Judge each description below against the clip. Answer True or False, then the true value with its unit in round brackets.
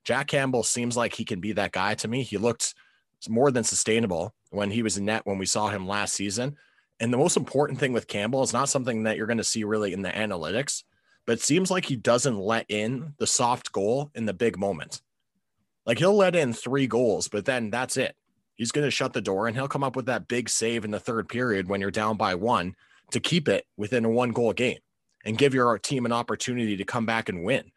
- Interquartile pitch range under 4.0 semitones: True (3.4 semitones)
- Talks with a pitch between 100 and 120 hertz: True (115 Hz)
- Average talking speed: False (245 wpm)